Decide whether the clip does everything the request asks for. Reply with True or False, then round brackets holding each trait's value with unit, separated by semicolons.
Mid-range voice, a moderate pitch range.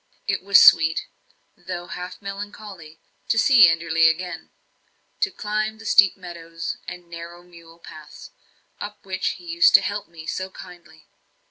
True (180 Hz; 3.6 semitones)